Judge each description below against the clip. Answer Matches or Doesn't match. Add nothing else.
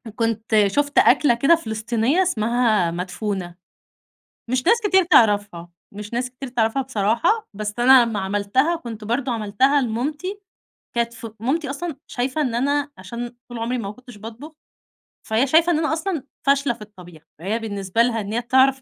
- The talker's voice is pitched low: Doesn't match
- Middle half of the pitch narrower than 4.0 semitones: Doesn't match